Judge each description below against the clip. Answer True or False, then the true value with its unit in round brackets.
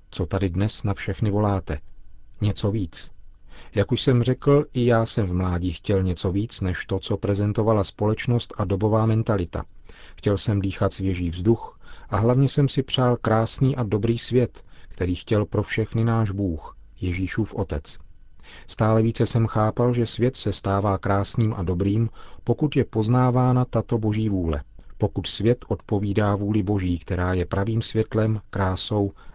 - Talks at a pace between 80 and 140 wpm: False (155 wpm)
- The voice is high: False (105 Hz)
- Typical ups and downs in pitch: True (3.1 semitones)